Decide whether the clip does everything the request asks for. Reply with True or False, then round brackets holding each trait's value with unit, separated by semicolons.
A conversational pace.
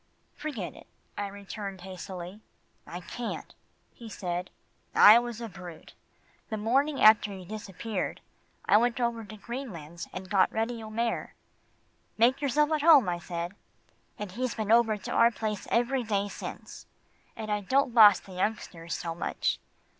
True (155 wpm)